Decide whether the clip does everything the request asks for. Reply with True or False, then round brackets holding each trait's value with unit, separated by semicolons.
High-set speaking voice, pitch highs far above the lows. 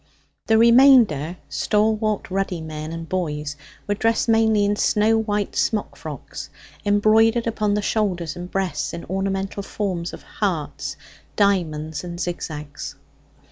False (195 Hz; 4.2 semitones)